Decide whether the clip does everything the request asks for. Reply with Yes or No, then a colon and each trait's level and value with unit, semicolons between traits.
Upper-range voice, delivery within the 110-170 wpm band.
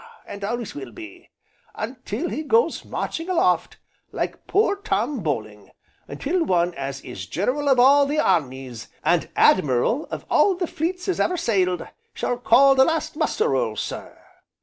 Yes: high, 245 Hz; average, 155 wpm